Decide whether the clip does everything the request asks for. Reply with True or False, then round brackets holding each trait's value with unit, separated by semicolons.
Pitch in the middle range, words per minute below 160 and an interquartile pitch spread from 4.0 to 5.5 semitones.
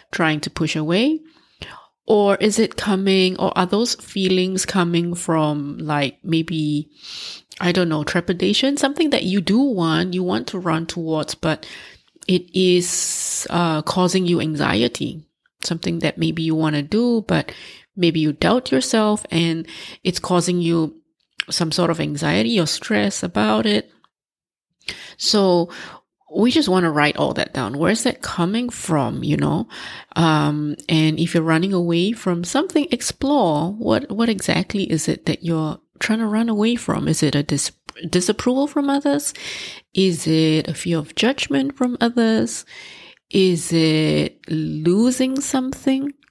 True (175 Hz; 150 wpm; 5.2 semitones)